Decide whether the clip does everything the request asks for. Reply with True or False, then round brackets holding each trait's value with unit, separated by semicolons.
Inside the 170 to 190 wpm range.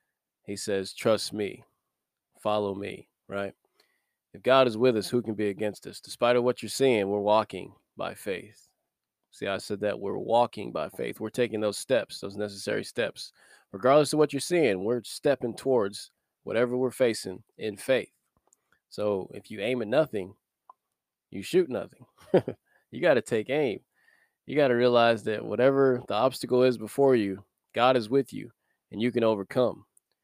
True (175 wpm)